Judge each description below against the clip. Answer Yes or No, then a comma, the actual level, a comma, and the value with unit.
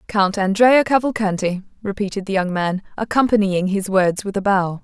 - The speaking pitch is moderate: No, high, 200 Hz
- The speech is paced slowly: No, average, 160 wpm